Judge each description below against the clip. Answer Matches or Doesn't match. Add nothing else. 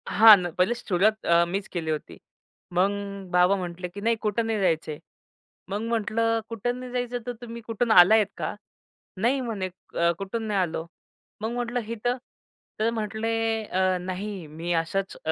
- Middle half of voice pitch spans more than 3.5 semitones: Matches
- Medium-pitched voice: Doesn't match